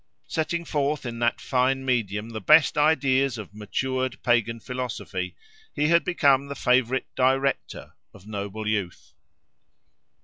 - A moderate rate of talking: No, slow, 130 wpm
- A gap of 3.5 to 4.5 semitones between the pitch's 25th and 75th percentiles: Yes, average, 4.1 semitones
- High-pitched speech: No, low, 130 Hz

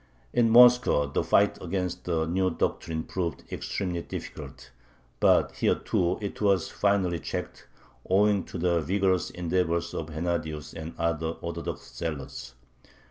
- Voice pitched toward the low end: Yes, very low, 85 Hz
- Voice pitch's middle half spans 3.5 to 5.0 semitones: No, average, 2.8 semitones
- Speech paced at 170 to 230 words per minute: No, slow, 135 wpm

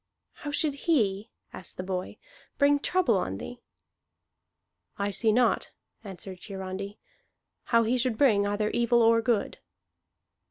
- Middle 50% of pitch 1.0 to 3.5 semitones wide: No, average, 3.9 semitones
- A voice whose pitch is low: No, high, 220 Hz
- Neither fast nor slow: No, slow, 130 wpm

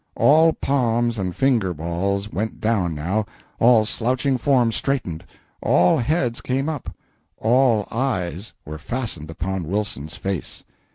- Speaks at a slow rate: Yes, slow, 125 wpm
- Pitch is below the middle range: Yes, low, 110 Hz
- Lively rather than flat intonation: Yes, wide, 6.0 semitones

